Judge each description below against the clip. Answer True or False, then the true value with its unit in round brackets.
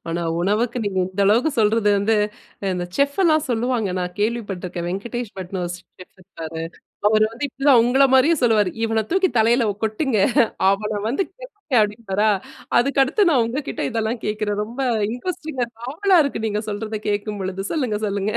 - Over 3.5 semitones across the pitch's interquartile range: True (4.0 semitones)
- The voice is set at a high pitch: True (220 Hz)